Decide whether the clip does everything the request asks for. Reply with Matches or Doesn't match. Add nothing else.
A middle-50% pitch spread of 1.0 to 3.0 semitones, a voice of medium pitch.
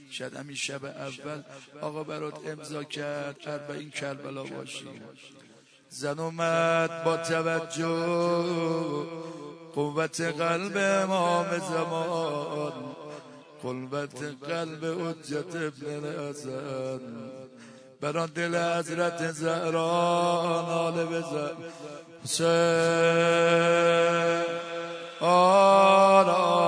Matches